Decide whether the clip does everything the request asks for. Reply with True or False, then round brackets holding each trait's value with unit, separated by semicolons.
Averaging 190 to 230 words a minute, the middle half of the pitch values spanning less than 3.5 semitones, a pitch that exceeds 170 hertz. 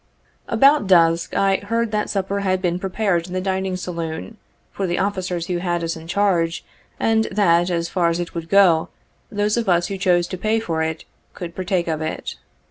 True (200 wpm; 2.9 semitones; 185 Hz)